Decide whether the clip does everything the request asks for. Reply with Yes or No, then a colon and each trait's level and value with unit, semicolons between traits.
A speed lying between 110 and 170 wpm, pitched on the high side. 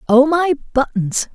Yes: slow, 135 wpm; very high, 275 Hz